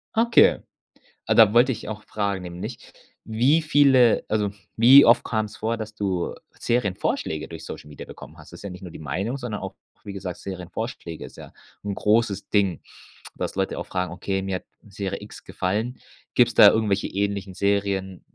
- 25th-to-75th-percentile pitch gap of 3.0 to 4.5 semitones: Yes, average, 3.3 semitones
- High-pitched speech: No, low, 100 Hz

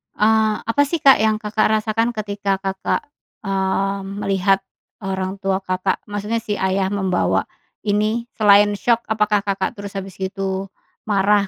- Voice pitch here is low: No, high, 200 Hz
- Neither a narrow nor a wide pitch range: No, narrow, 1.9 semitones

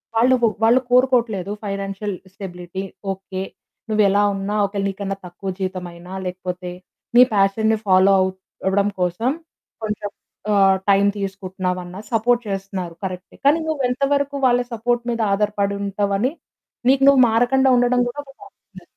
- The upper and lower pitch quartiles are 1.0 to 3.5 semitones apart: No, average, 4.0 semitones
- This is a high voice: Yes, high, 200 Hz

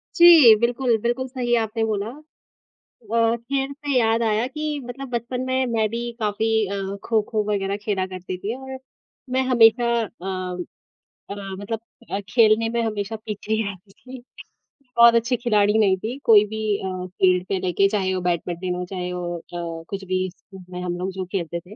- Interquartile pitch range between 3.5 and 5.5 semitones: Yes, average, 4.0 semitones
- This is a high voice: Yes, high, 215 Hz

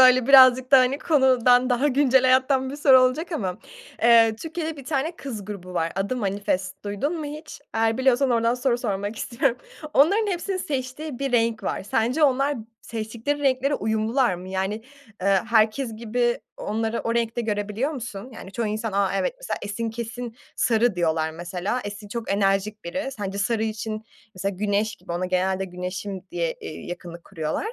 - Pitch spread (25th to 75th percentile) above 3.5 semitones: Yes, average, 4.6 semitones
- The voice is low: No, high, 230 Hz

